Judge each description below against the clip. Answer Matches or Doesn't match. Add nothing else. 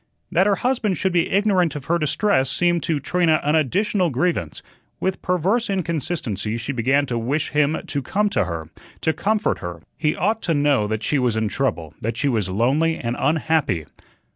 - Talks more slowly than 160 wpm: Doesn't match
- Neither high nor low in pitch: Matches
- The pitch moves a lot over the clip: Matches